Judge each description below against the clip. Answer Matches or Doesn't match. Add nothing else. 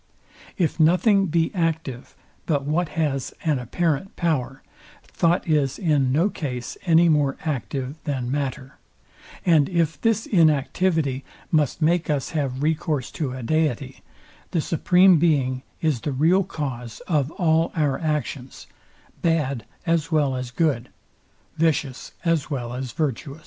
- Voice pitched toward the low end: Doesn't match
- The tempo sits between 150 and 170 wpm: Doesn't match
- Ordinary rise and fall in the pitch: Matches